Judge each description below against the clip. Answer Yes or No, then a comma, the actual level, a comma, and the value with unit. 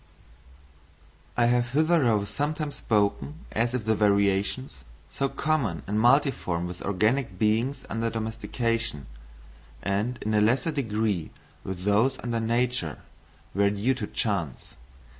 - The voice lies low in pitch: Yes, low, 115 Hz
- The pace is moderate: No, slow, 115 wpm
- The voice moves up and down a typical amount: Yes, average, 4.1 semitones